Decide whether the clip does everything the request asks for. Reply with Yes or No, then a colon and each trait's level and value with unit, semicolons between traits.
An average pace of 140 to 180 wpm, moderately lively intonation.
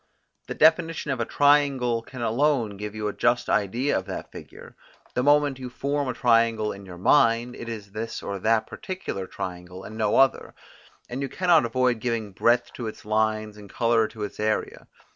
No: average, 190 wpm; average, 3.6 semitones